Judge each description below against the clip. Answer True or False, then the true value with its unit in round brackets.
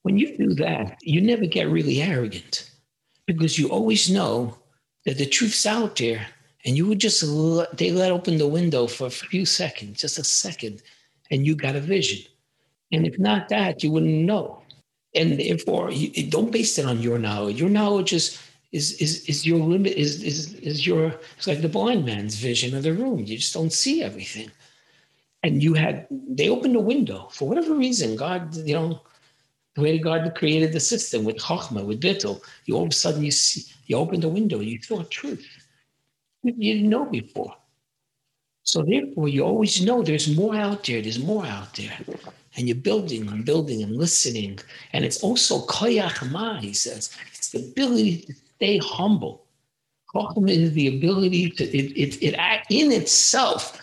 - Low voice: False (160 Hz)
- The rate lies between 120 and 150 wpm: False (185 wpm)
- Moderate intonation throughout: False (6.1 semitones)